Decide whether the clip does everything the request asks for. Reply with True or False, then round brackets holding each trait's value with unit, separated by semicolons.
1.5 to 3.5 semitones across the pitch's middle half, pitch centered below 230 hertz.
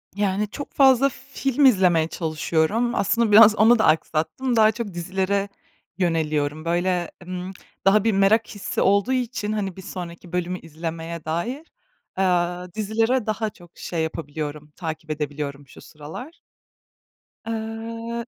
False (5.2 semitones; 190 Hz)